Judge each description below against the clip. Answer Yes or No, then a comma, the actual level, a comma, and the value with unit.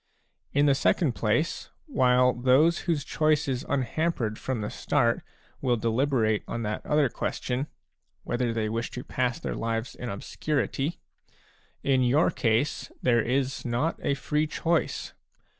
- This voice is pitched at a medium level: No, low, 125 Hz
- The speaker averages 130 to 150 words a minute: Yes, average, 140 wpm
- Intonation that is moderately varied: Yes, average, 3.9 semitones